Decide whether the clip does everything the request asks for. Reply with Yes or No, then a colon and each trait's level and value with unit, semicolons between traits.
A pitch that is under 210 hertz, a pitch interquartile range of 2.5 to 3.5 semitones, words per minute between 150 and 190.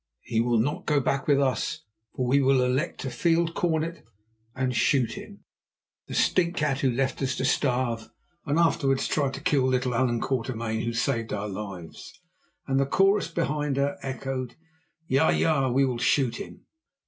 Yes: low, 135 Hz; average, 3.0 semitones; average, 165 wpm